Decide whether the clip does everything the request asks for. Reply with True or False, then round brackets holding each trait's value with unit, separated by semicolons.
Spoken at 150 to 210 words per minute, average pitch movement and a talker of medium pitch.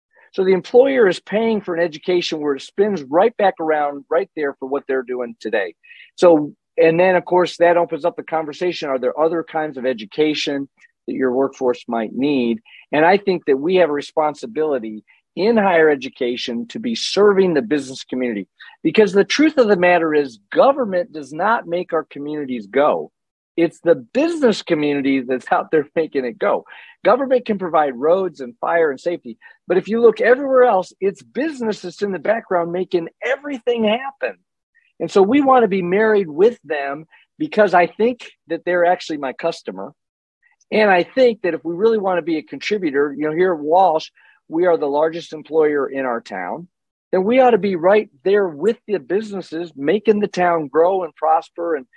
False (190 wpm; 5.8 semitones; 175 Hz)